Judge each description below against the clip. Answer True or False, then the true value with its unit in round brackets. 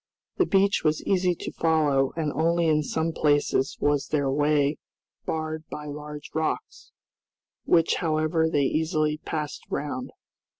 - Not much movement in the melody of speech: True (1.6 semitones)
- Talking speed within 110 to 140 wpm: True (135 wpm)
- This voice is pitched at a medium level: True (155 Hz)